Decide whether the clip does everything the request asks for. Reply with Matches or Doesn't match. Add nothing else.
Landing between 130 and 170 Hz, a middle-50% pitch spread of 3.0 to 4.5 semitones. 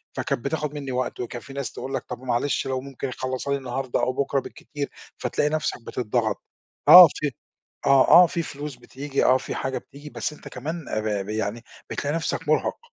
Doesn't match